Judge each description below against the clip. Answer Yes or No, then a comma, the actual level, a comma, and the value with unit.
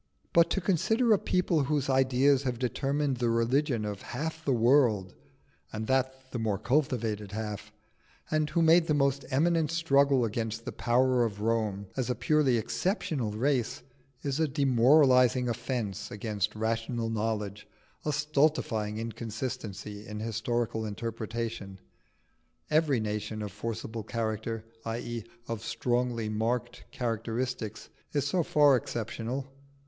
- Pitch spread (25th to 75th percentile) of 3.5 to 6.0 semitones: Yes, average, 3.9 semitones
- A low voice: Yes, low, 120 Hz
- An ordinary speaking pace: No, slow, 130 wpm